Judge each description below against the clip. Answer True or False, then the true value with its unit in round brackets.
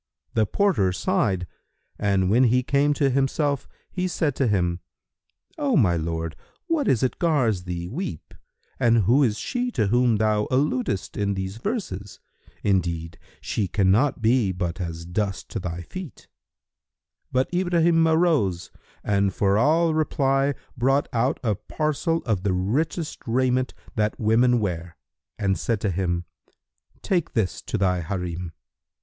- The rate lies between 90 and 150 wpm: True (145 wpm)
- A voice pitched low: True (110 Hz)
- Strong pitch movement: True (7.1 semitones)